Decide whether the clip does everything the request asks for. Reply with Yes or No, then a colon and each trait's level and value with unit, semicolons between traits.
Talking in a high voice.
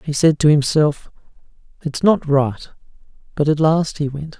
No: medium, 150 Hz